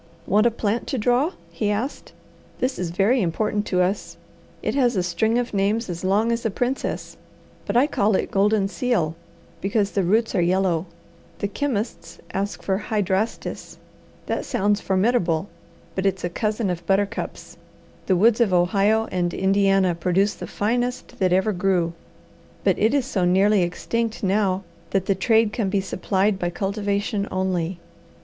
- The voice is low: No, high, 200 Hz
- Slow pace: No, average, 160 wpm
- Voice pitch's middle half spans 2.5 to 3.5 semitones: Yes, average, 3.0 semitones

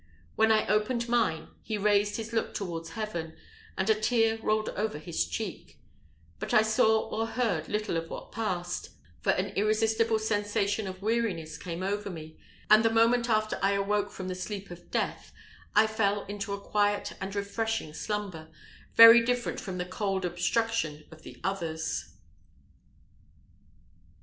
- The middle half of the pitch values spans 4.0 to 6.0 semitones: No, average, 3.2 semitones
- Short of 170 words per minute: Yes, average, 155 wpm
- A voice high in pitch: Yes, high, 205 Hz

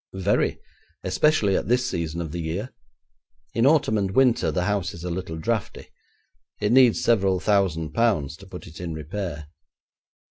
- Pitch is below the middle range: Yes, very low, 95 Hz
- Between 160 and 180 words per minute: Yes, average, 165 wpm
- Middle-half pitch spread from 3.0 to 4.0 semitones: No, average, 5.2 semitones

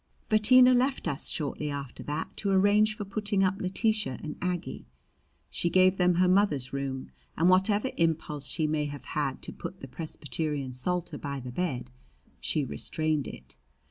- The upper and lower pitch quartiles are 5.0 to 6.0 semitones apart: Yes, average, 5.3 semitones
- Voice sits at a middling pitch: Yes, medium, 170 Hz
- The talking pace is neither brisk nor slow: Yes, average, 165 wpm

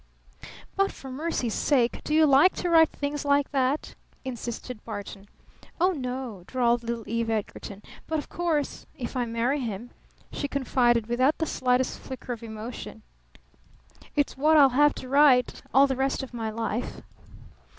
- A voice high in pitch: Yes, very high, 255 Hz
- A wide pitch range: No, average, 3.5 semitones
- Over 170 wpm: No, average, 160 wpm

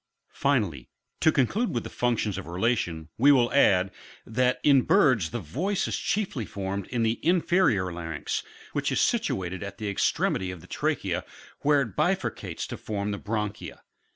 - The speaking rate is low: No, average, 165 wpm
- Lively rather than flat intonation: Yes, wide, 6.2 semitones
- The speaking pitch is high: No, low, 110 Hz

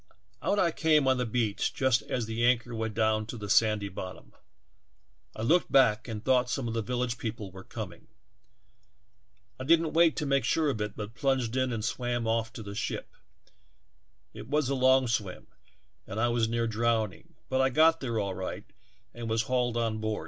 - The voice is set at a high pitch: No, low, 115 Hz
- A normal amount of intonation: Yes, average, 3.1 semitones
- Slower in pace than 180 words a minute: Yes, average, 165 wpm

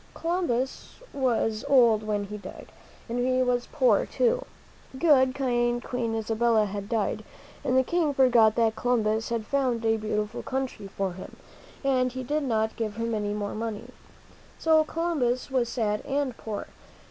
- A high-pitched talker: Yes, high, 240 Hz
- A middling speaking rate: Yes, average, 160 wpm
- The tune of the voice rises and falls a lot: No, average, 3.2 semitones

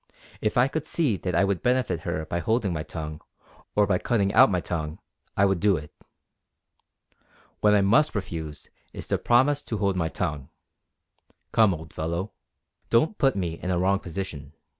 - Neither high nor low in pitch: No, very low, 95 Hz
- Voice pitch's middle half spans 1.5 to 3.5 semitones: No, average, 5.1 semitones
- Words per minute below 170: No, average, 180 wpm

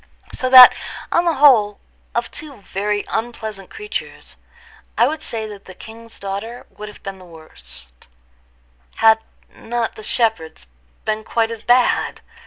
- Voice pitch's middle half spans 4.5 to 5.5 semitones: No, average, 2.8 semitones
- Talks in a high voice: Yes, high, 220 Hz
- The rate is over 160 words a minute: No, average, 145 wpm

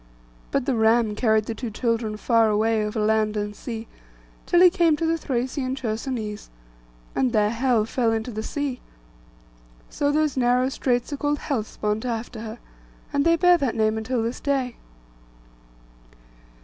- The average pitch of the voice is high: Yes, high, 235 Hz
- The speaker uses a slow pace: No, average, 160 wpm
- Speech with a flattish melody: No, average, 3.7 semitones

